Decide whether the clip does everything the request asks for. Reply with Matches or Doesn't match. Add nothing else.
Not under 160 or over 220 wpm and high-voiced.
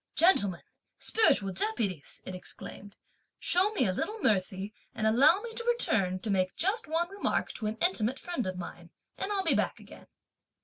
Matches